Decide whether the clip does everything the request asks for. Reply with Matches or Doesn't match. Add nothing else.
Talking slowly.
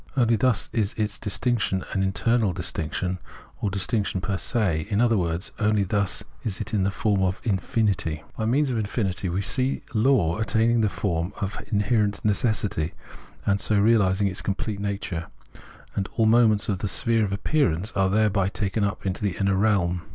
Doesn't match